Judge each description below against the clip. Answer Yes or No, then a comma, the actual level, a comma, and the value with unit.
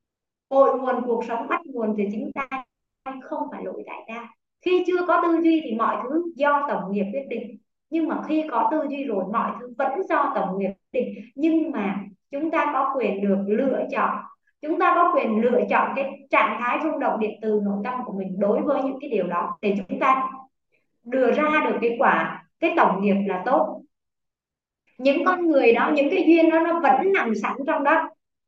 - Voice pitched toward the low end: No, very high, 265 Hz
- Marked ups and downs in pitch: Yes, wide, 5.7 semitones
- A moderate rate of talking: Yes, average, 215 wpm